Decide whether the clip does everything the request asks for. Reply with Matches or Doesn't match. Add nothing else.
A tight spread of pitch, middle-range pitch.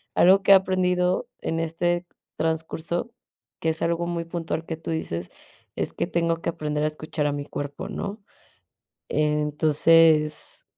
Matches